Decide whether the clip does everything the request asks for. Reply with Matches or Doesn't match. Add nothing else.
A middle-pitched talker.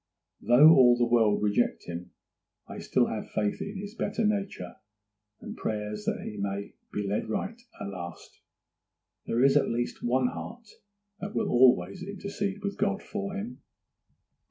Doesn't match